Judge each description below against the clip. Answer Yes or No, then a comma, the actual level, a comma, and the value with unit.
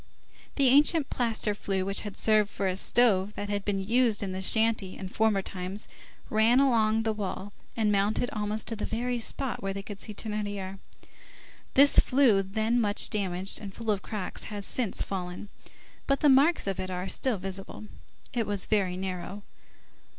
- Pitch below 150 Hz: No, high, 210 Hz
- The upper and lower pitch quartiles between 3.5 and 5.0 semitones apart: No, average, 2.7 semitones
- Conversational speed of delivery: Yes, average, 180 wpm